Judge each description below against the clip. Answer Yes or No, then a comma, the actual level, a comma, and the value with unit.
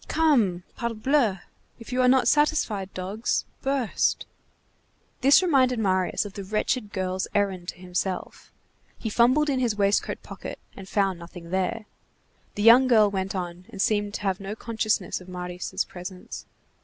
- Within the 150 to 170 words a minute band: Yes, average, 155 wpm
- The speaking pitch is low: No, high, 205 Hz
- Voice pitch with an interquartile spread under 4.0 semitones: No, average, 4.5 semitones